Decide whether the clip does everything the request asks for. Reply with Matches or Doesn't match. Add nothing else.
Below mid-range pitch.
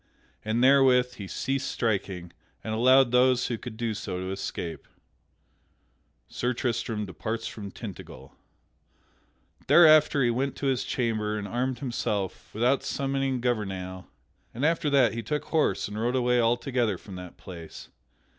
Matches